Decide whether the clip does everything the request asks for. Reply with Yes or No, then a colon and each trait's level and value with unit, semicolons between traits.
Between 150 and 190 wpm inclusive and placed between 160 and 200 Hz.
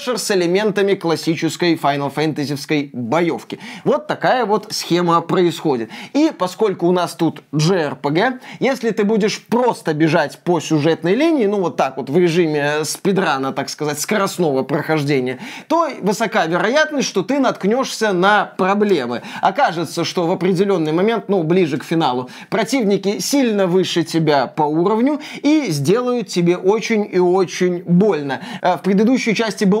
No: average, 140 wpm; medium, 185 Hz